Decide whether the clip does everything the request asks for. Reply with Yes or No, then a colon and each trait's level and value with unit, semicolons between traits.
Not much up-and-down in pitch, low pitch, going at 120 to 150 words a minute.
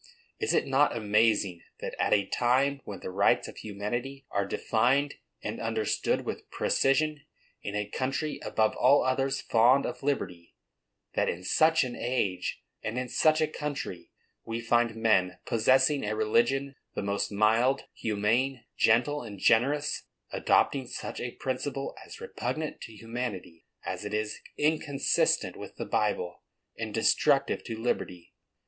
No: average, 4.4 semitones; low, 120 Hz; average, 145 wpm